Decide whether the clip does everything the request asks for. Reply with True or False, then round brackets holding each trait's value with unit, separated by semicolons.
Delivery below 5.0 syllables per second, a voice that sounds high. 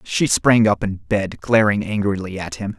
False (4.5 syllables/s; 105 Hz)